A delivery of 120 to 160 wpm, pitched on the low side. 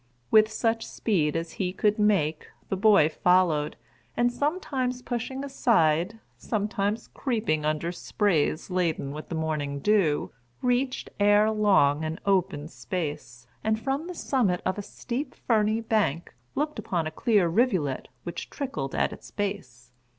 No: average, 145 wpm; high, 200 Hz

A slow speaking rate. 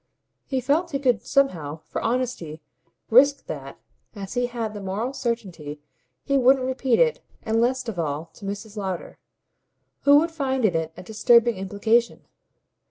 No: average, 160 wpm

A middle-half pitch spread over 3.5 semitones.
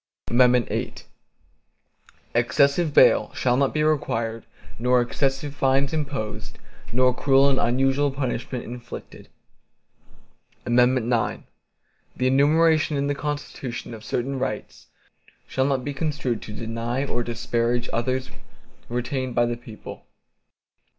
No: average, 2.7 semitones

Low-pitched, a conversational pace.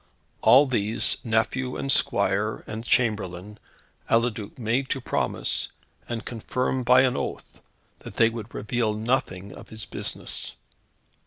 No: low, 115 Hz; slow, 130 wpm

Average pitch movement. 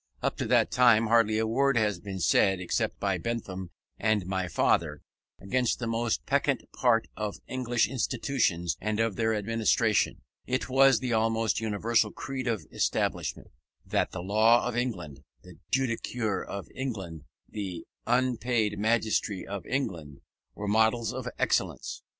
Yes: average, 3.2 semitones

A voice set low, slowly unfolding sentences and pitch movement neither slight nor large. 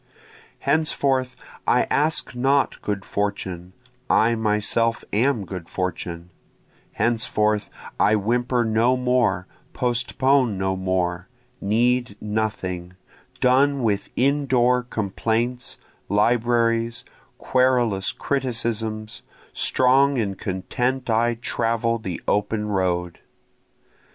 Yes: low, 115 Hz; slow, 90 wpm; average, 3.7 semitones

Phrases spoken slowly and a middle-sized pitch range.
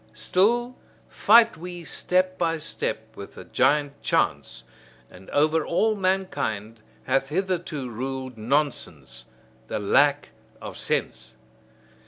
No: slow, 110 wpm; wide, 8.3 semitones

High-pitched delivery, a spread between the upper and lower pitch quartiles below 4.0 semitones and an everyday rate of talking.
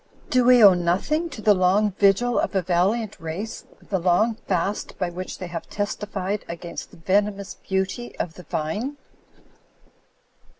Yes: high, 195 Hz; average, 3.2 semitones; average, 155 wpm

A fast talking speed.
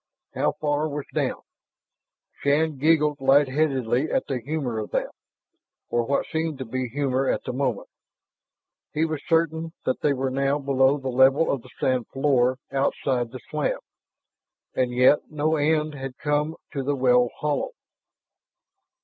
No: average, 150 wpm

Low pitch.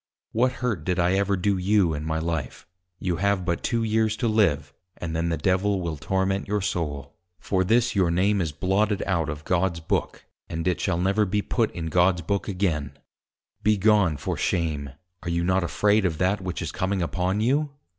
Yes: very low, 95 Hz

